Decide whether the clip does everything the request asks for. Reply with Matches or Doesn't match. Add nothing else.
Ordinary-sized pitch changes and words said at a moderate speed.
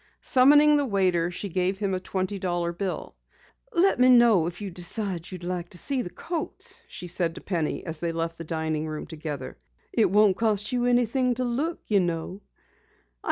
Doesn't match